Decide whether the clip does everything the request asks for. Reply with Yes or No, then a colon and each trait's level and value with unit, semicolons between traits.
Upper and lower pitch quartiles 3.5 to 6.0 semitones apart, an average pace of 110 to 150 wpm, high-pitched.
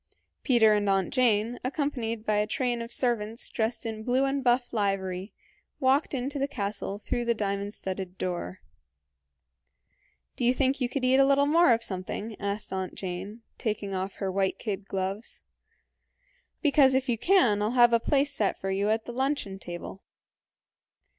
No: average, 4.5 semitones; average, 170 wpm; high, 225 Hz